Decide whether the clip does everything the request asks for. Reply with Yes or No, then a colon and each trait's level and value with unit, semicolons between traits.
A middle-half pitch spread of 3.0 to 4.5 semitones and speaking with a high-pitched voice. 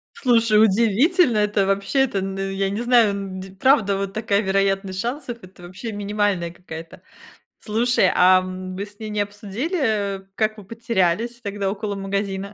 No: narrow, 2.6 semitones; high, 200 Hz